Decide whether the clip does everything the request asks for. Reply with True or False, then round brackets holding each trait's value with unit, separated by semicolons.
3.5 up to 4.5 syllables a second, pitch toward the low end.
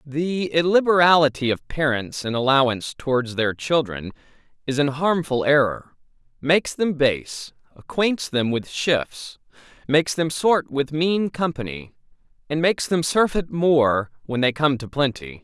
False (4.4 syllables/s; 145 Hz)